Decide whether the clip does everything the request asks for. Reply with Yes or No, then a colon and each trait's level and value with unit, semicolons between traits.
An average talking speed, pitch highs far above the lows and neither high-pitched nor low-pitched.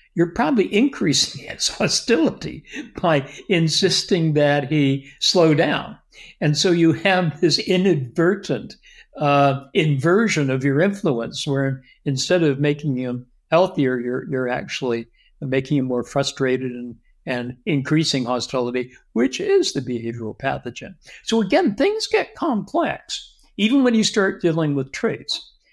No: slow, 130 wpm; wide, 5.9 semitones; medium, 145 Hz